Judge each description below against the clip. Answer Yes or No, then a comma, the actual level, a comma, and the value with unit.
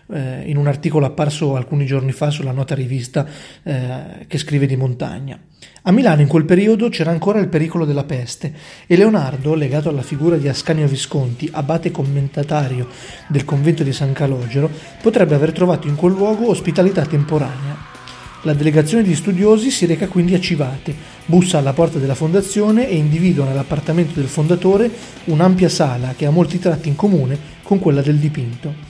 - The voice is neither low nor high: Yes, medium, 155 Hz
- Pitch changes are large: No, average, 3.8 semitones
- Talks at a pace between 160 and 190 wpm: Yes, average, 165 wpm